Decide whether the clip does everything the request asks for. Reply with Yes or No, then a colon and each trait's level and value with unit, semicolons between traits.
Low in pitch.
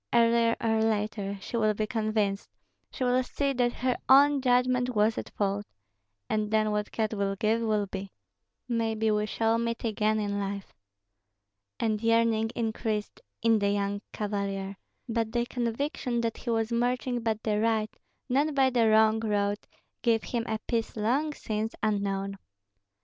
No: high, 220 Hz